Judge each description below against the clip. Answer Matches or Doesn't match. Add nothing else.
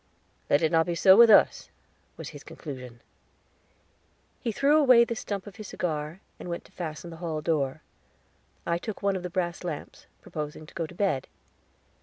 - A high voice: Doesn't match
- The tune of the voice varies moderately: Matches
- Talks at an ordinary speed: Matches